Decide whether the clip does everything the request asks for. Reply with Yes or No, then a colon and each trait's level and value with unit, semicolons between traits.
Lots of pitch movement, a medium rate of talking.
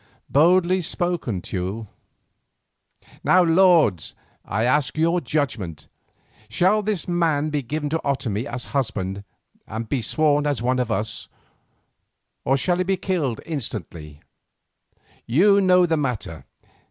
No: wide, 7.7 semitones; slow, 125 wpm